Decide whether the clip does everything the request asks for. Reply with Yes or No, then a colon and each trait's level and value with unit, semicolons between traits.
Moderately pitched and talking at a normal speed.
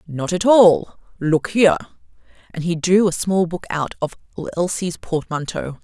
Yes: medium, 175 Hz; average, 155 wpm